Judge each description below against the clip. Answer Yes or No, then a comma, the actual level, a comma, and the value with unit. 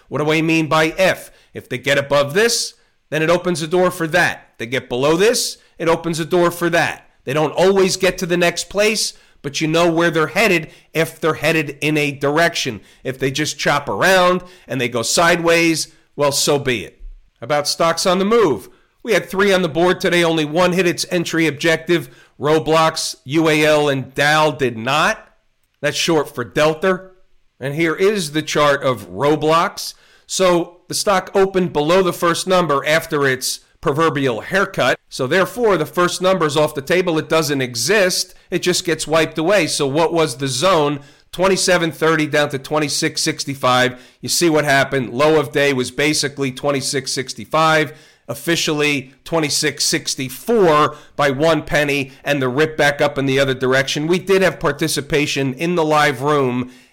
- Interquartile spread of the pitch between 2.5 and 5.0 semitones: Yes, average, 3.4 semitones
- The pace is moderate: Yes, average, 175 wpm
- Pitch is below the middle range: No, medium, 155 Hz